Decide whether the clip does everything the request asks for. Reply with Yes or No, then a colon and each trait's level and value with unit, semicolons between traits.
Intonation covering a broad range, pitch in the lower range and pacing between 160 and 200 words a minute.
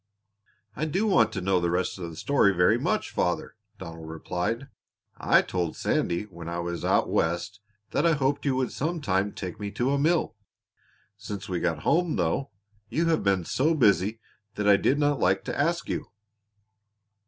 Yes: wide, 8.2 semitones; low, 105 Hz; average, 185 wpm